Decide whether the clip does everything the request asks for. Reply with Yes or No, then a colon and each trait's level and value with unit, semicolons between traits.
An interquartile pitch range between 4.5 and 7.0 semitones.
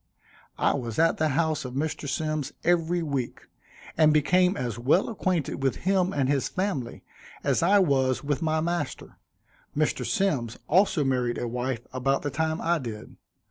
Yes: average, 4.8 semitones